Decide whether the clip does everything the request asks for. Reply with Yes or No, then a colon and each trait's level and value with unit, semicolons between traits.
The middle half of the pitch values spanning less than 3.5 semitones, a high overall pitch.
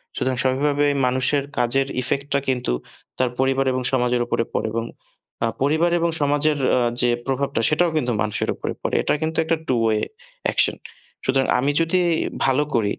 No: average, 2.8 semitones; low, 135 Hz